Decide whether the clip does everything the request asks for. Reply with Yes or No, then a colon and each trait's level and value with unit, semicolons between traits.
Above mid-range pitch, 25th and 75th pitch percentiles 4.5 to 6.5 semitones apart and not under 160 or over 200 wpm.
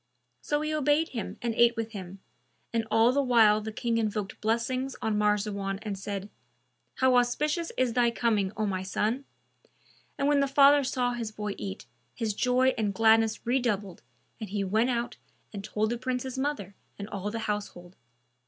No: high, 225 Hz; average, 3.5 semitones; average, 175 wpm